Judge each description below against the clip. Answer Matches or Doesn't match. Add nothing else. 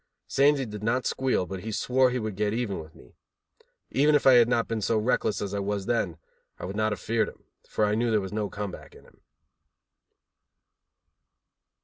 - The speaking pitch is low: Matches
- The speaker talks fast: Matches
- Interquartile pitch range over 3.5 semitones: Doesn't match